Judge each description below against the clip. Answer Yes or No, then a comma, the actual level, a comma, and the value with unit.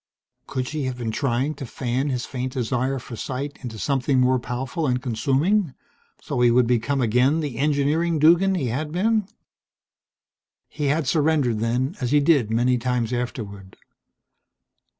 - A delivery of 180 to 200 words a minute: No, average, 155 wpm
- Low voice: Yes, low, 130 Hz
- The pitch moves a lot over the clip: No, average, 3.3 semitones